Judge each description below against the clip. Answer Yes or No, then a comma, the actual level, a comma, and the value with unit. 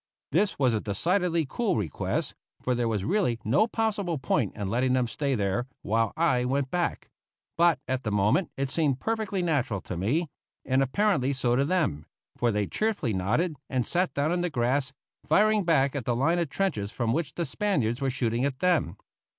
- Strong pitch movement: Yes, wide, 6.5 semitones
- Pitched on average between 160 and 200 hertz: No, low, 135 Hz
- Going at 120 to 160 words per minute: No, average, 190 wpm